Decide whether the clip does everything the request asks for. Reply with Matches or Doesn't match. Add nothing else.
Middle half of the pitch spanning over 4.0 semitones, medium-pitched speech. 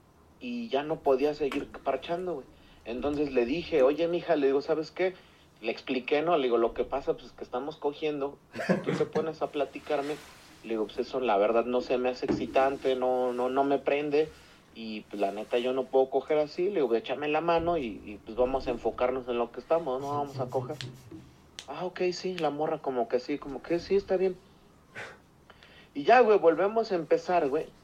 Matches